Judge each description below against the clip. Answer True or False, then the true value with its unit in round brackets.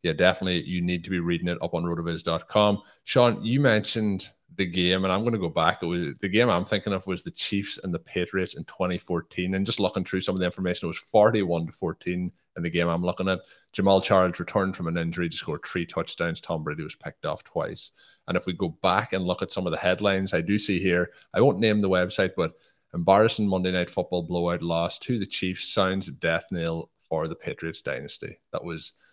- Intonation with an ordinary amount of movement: False (2.2 semitones)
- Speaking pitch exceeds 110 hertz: False (95 Hz)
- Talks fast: True (230 wpm)